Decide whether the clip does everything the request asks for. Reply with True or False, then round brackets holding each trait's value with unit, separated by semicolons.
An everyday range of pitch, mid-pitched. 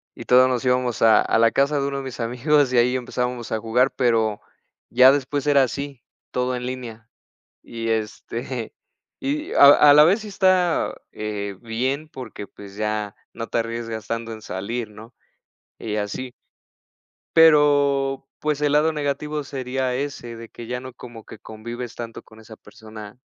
False (3.6 semitones; 125 Hz)